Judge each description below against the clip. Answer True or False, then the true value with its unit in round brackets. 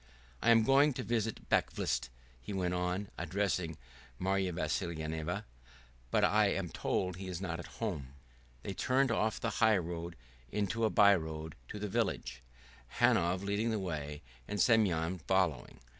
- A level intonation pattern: False (4.1 semitones)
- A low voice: True (95 Hz)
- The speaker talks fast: False (150 wpm)